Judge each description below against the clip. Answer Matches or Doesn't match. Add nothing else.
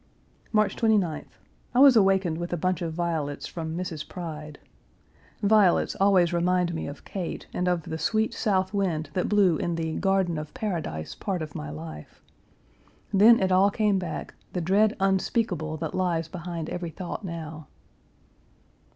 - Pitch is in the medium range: Matches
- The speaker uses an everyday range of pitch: Matches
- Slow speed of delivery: Doesn't match